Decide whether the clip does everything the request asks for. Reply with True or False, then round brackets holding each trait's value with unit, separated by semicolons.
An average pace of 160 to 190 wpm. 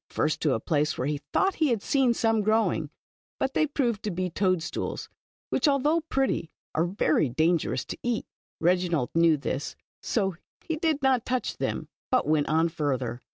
True (185 wpm)